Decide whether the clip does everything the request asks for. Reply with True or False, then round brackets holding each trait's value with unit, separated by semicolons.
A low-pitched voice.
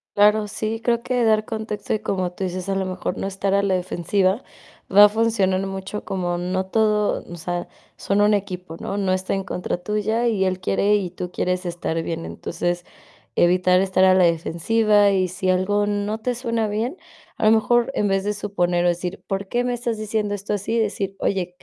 False (195 Hz)